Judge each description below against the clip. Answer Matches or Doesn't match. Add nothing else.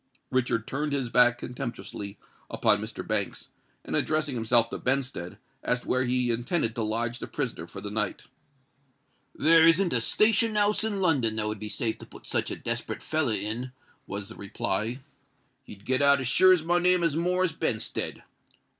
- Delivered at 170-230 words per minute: Matches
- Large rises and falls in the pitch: Matches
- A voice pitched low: Matches